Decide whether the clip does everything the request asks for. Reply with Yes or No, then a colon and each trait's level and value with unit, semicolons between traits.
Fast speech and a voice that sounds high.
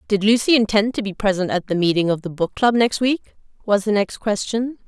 Yes: fast, 235 wpm; high, 210 Hz